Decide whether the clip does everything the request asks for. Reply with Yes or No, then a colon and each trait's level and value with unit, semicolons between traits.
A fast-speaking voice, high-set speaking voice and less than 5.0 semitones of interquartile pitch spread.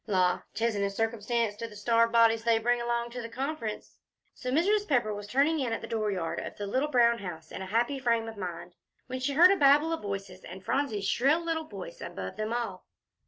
Yes: fast, 215 wpm; high, 230 Hz; average, 4.2 semitones